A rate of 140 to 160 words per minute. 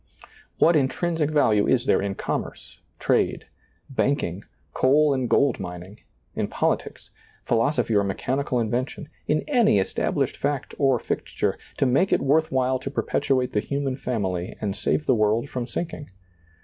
Yes: average, 150 wpm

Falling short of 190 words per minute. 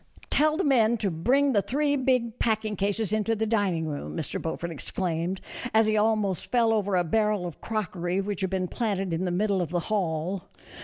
No: average, 200 wpm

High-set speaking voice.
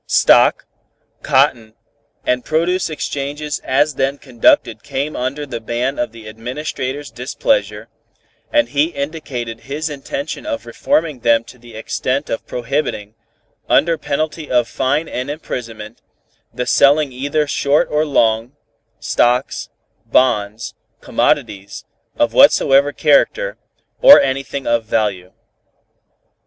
No: low, 135 Hz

